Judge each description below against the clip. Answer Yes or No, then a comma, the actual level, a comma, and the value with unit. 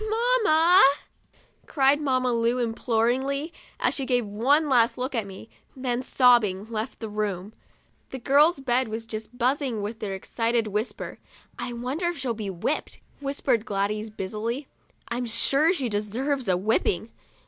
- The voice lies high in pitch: Yes, high, 240 Hz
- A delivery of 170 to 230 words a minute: No, average, 160 wpm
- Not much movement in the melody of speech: No, average, 4.0 semitones